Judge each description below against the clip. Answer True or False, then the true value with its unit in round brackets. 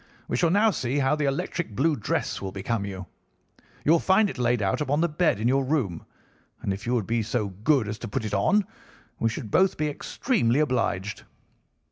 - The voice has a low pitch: True (125 Hz)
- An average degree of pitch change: False (6.4 semitones)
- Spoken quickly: True (210 wpm)